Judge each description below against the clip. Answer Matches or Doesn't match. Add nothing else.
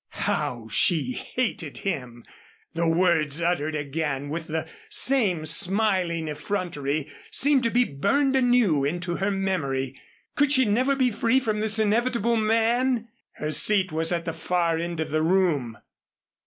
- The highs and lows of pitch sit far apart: Matches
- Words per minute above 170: Doesn't match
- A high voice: Doesn't match